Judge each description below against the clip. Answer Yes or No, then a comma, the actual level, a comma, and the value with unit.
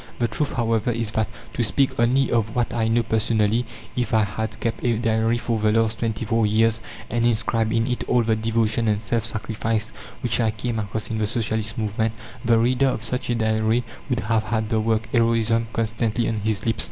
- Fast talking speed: Yes, fast, 210 wpm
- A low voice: Yes, low, 115 Hz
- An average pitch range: No, narrow, 1.1 semitones